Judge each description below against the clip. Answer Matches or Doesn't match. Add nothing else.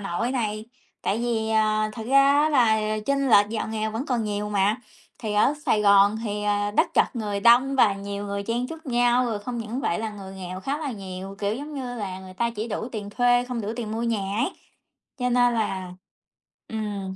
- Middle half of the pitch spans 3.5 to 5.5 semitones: Doesn't match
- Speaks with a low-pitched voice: Doesn't match